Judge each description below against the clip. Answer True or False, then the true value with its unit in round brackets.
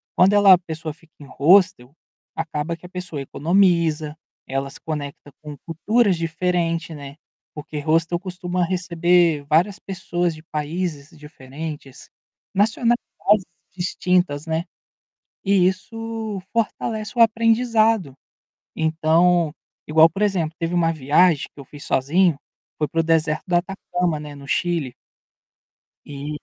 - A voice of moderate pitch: True (165 Hz)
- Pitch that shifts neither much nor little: True (3.4 semitones)